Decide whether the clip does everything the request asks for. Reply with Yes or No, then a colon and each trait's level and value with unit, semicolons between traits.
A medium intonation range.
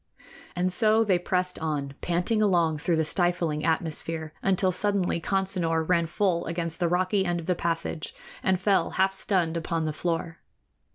No: narrow, 2.3 semitones